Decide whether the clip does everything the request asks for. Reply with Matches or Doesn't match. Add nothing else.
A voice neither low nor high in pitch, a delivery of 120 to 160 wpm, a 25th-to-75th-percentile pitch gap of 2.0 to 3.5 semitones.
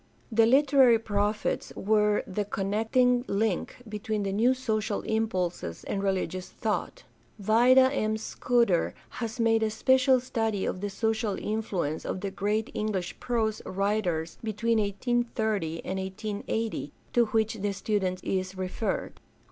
Doesn't match